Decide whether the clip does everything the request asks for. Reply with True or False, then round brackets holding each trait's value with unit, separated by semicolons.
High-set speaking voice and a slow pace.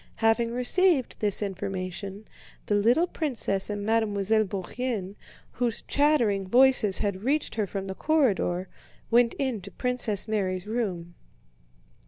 True (215 Hz; 120 wpm)